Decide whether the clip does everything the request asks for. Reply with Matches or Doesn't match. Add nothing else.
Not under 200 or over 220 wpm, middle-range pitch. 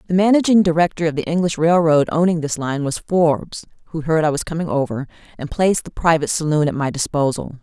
Matches